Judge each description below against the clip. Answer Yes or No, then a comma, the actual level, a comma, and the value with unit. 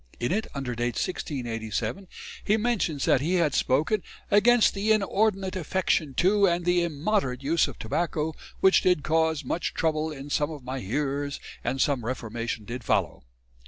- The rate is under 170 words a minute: Yes, average, 160 wpm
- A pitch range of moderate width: No, wide, 6.0 semitones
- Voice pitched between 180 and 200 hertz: No, medium, 155 Hz